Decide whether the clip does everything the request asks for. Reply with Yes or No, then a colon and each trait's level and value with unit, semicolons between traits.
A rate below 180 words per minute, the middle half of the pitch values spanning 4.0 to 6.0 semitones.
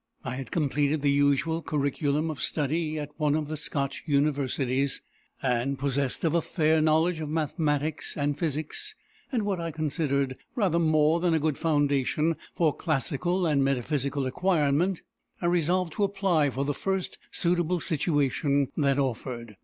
No: average, 155 wpm; average, 3.0 semitones